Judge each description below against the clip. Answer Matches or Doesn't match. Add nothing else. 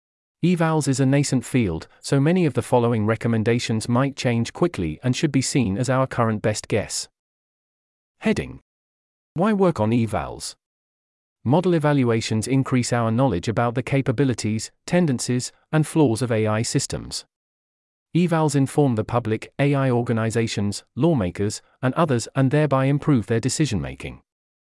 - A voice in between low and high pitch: Doesn't match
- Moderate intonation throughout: Matches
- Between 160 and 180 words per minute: Doesn't match